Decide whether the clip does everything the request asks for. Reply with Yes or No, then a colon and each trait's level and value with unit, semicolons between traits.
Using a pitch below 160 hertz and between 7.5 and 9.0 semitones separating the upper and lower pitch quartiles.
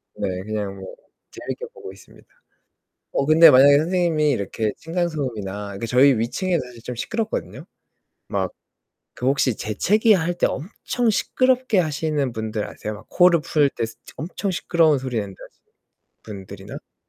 Yes: medium, 140 Hz; wide, 8.0 semitones